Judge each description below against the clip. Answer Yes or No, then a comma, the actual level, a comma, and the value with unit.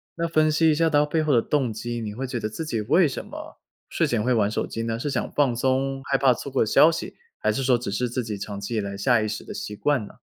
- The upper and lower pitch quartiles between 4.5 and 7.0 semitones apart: Yes, average, 4.8 semitones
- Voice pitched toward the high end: No, low, 125 Hz